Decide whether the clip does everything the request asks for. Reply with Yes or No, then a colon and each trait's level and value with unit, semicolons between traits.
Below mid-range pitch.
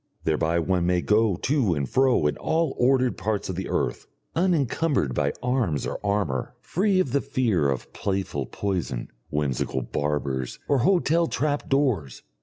Yes: low, 100 Hz